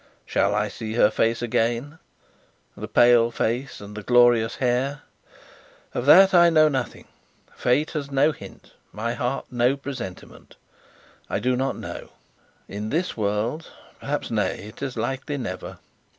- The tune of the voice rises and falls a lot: No, average, 3.7 semitones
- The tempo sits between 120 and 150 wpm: Yes, average, 145 wpm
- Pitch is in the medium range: No, low, 125 Hz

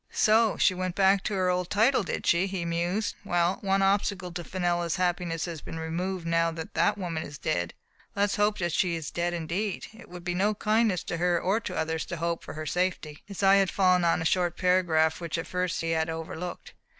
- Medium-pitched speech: Yes, medium, 180 Hz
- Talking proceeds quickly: Yes, fast, 225 wpm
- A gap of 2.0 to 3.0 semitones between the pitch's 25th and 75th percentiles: Yes, narrow, 2.5 semitones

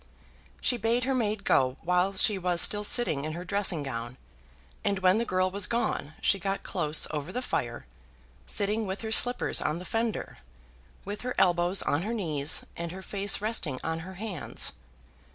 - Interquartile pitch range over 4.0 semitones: Yes, average, 4.7 semitones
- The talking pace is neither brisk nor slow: Yes, average, 180 wpm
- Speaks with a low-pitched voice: No, high, 190 Hz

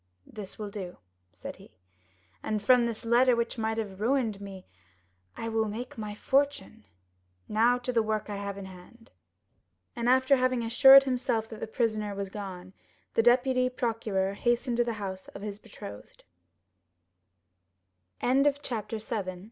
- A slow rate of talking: No, average, 155 wpm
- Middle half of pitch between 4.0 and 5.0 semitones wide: No, average, 3.4 semitones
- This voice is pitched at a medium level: No, high, 225 Hz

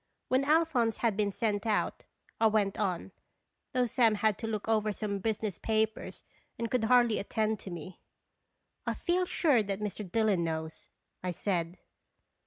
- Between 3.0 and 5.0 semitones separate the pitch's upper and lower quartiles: No, narrow, 2.6 semitones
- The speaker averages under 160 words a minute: No, average, 165 wpm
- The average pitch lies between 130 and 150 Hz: No, high, 215 Hz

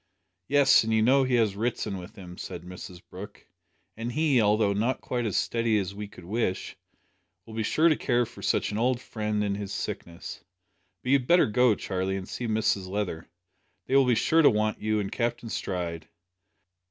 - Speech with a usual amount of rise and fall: Yes, average, 3.7 semitones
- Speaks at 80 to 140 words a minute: No, average, 195 wpm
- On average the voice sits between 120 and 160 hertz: No, low, 110 Hz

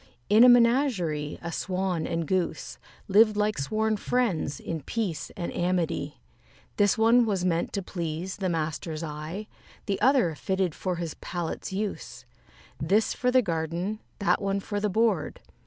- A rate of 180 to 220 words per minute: No, average, 155 wpm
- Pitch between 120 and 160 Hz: No, high, 190 Hz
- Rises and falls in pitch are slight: No, average, 4.5 semitones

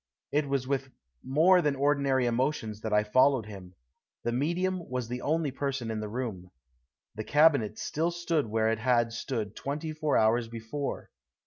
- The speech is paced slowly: No, average, 165 wpm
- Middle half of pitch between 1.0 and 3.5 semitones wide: No, average, 4.7 semitones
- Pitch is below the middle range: Yes, low, 130 Hz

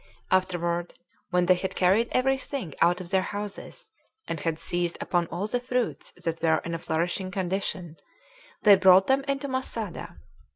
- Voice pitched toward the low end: No, medium, 185 Hz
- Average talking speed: Yes, average, 165 wpm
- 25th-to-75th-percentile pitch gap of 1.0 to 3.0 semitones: No, average, 3.6 semitones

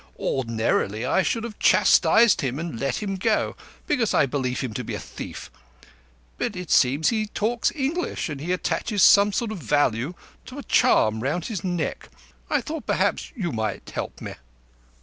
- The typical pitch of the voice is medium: Yes, medium, 175 Hz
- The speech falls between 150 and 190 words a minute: Yes, average, 175 wpm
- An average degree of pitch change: No, wide, 9.0 semitones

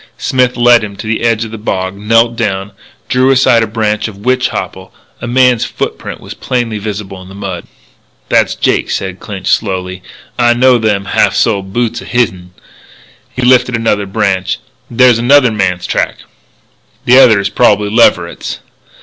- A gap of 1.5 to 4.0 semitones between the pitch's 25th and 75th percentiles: Yes, average, 3.6 semitones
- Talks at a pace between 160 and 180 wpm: Yes, average, 165 wpm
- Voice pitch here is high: No, low, 110 Hz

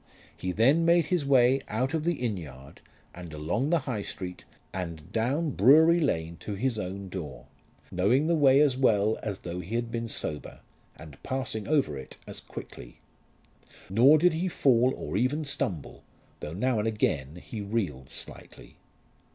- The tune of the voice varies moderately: No, wide, 7.5 semitones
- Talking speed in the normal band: Yes, average, 170 wpm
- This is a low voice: Yes, low, 110 Hz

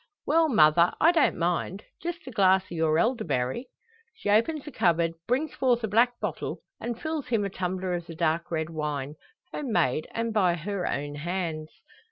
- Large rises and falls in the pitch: Yes, wide, 6.7 semitones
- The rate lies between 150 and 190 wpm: Yes, average, 185 wpm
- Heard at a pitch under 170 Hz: No, medium, 185 Hz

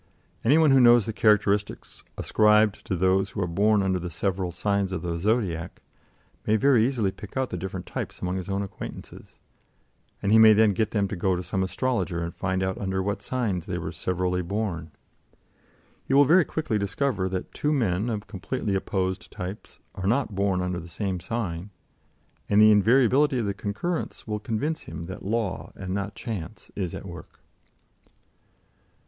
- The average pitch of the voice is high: No, low, 100 Hz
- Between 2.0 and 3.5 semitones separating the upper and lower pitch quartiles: Yes, average, 3.2 semitones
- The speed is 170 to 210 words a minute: Yes, average, 180 wpm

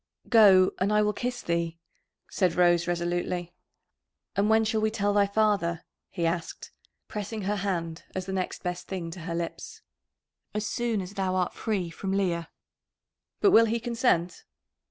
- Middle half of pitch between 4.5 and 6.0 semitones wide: No, average, 3.4 semitones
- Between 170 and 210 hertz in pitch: Yes, high, 190 Hz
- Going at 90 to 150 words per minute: No, average, 165 wpm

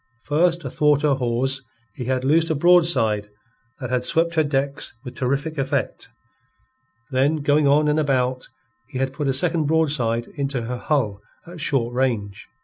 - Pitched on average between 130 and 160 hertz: Yes, medium, 140 Hz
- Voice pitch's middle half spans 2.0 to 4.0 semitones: Yes, average, 3.3 semitones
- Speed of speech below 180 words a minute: Yes, average, 160 wpm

